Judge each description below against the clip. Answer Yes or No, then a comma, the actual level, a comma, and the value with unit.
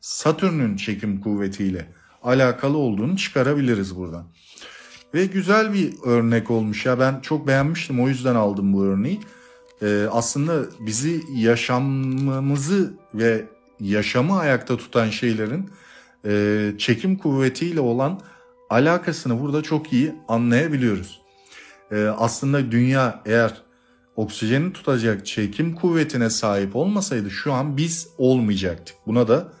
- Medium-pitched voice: No, low, 125 Hz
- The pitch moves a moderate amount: No, wide, 6.1 semitones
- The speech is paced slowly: No, average, 110 wpm